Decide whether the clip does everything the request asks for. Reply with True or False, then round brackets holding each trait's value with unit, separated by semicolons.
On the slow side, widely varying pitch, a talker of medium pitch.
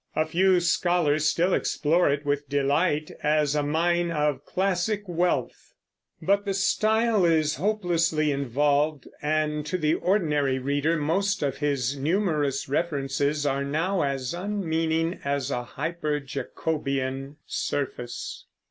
False (125 wpm; 3.5 semitones; 155 Hz)